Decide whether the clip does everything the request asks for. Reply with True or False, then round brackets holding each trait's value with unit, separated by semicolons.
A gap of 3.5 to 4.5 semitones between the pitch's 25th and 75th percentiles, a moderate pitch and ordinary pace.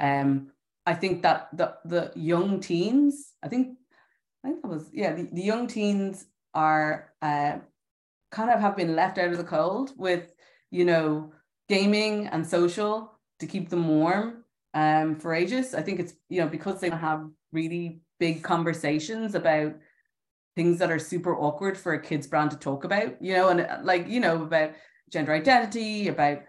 True (4.1 semitones; 175 Hz; 175 wpm)